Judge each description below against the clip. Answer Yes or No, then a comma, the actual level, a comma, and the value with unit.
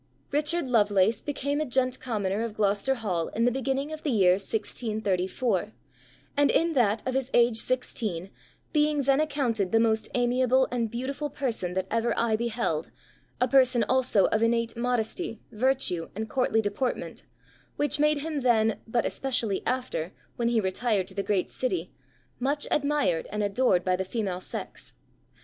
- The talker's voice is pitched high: Yes, high, 235 Hz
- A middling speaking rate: Yes, average, 165 wpm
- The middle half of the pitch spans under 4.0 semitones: No, average, 4.3 semitones